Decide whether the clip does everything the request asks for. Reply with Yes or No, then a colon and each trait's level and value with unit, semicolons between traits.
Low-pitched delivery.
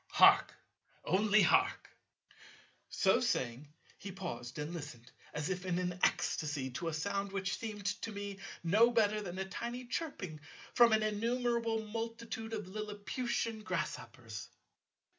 No: high, 200 Hz